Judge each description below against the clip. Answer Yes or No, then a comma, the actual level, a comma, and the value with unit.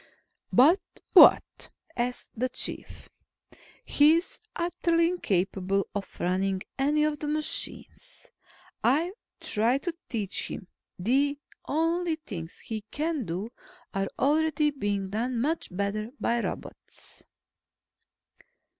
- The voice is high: Yes, very high, 255 Hz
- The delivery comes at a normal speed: No, slow, 105 wpm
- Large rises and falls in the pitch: Yes, wide, 7.4 semitones